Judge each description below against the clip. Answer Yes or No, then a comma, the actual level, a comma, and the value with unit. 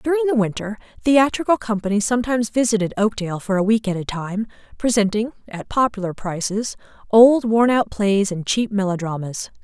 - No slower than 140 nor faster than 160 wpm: Yes, average, 155 wpm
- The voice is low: No, high, 215 Hz